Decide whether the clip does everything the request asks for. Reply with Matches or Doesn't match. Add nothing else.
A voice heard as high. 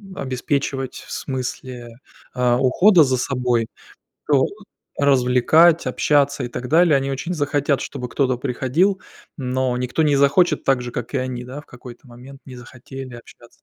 Doesn't match